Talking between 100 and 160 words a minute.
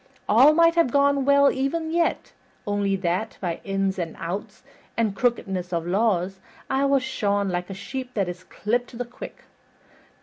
No: average, 170 wpm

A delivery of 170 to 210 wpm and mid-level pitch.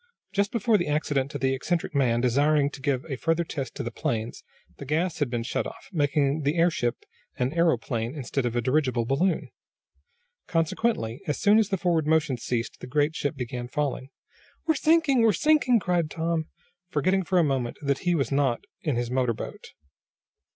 Yes: average, 185 wpm; medium, 145 Hz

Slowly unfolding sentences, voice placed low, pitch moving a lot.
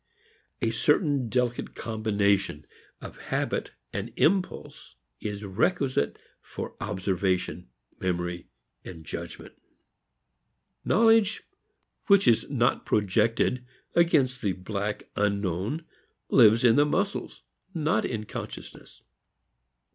Yes: slow, 95 wpm; low, 110 Hz; wide, 6.1 semitones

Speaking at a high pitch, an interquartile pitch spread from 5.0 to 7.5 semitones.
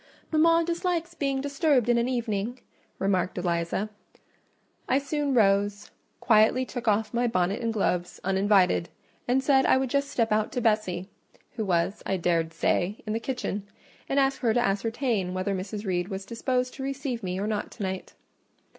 Yes: high, 220 Hz; average, 5.3 semitones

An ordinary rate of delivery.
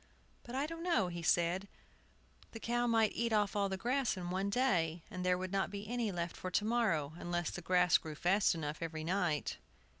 No: fast, 215 wpm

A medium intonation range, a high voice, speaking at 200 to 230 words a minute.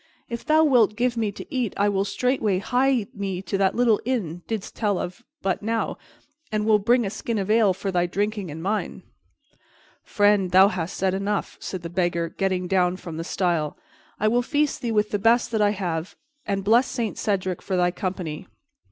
Yes: average, 3.5 semitones; high, 200 Hz; fast, 205 wpm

